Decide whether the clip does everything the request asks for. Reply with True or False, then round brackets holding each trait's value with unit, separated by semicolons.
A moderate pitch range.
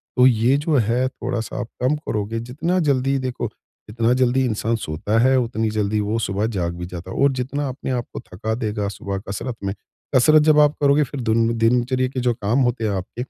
True (3.2 semitones)